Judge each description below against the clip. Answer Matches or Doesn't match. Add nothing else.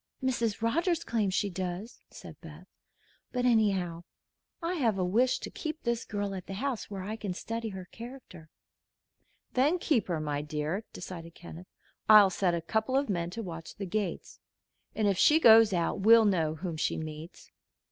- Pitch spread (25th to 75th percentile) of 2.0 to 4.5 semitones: Doesn't match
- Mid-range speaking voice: Doesn't match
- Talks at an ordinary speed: Matches